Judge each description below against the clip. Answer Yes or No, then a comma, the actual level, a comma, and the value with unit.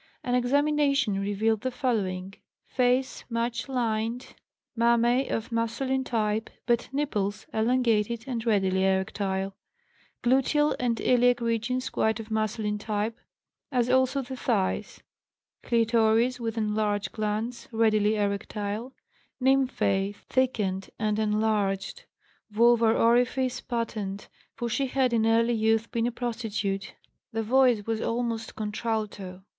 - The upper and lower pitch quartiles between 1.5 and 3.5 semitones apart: Yes, average, 2.8 semitones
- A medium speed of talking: No, slow, 115 wpm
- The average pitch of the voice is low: No, high, 225 Hz